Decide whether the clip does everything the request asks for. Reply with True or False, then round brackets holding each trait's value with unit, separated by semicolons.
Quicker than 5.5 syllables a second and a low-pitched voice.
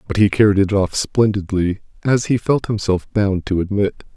False (4.9 syllables/s; 100 Hz)